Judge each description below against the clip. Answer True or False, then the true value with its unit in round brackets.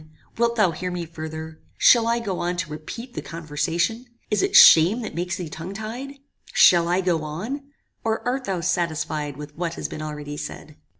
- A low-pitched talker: False (175 Hz)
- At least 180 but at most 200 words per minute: True (190 wpm)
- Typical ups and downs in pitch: False (5.8 semitones)